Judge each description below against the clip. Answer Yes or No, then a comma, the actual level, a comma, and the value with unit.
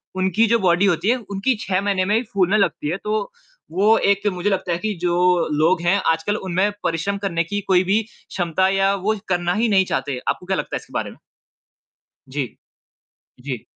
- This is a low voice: No, high, 190 Hz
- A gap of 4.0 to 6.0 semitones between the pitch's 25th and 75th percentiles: No, narrow, 2.6 semitones